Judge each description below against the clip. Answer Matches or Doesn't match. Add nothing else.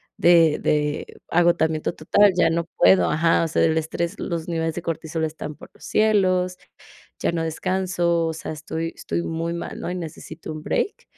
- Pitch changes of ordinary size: Doesn't match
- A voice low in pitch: Doesn't match